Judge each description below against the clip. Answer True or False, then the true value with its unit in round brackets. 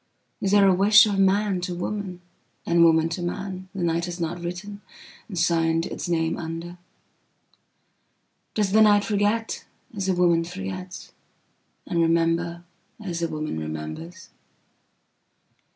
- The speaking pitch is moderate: True (175 Hz)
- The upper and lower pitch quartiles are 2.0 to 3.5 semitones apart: True (2.7 semitones)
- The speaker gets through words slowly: True (105 wpm)